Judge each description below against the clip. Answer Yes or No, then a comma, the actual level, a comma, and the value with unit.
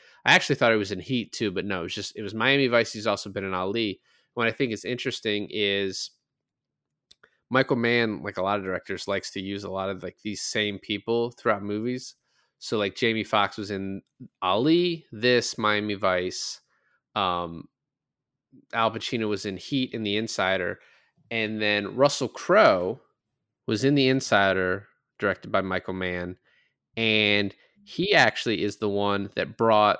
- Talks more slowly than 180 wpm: Yes, average, 170 wpm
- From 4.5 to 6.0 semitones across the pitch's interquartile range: No, average, 2.9 semitones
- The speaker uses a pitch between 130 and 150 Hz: No, low, 105 Hz